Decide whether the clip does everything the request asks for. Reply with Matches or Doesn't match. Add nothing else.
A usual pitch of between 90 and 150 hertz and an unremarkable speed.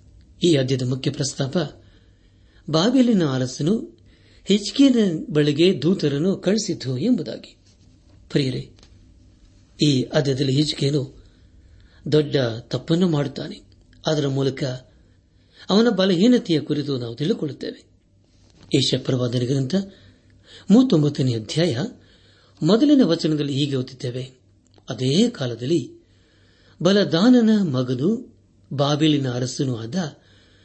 Matches